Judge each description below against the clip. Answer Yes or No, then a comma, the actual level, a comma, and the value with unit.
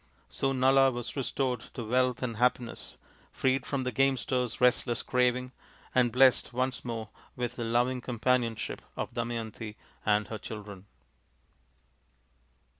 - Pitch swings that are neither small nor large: No, narrow, 1.8 semitones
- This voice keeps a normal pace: No, slow, 125 wpm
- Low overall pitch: Yes, low, 125 Hz